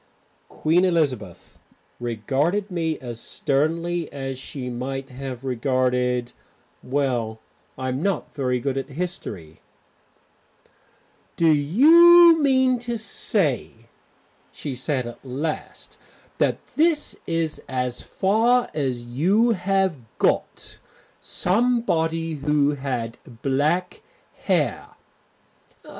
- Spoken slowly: Yes, slow, 95 wpm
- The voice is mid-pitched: Yes, medium, 145 Hz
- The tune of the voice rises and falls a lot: Yes, wide, 6.3 semitones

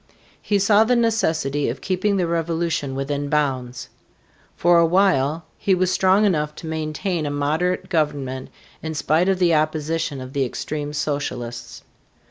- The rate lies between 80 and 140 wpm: No, average, 150 wpm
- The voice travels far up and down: No, average, 4.2 semitones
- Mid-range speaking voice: Yes, medium, 155 Hz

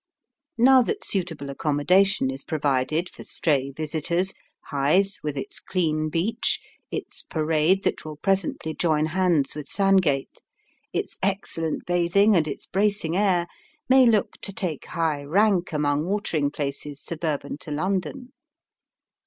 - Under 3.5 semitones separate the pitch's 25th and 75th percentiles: No, average, 4.6 semitones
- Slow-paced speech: Yes, slow, 130 wpm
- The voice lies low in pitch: No, medium, 165 Hz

